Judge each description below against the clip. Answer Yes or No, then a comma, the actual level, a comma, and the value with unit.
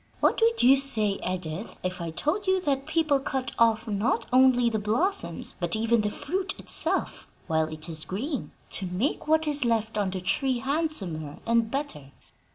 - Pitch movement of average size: No, wide, 7.2 semitones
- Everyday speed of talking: Yes, average, 175 wpm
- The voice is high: Yes, high, 230 Hz